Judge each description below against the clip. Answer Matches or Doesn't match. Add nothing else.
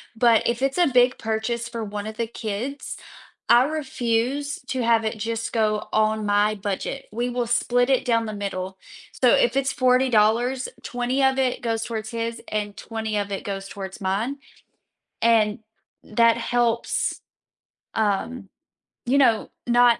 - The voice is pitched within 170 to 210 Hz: Doesn't match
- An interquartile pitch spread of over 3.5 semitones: Doesn't match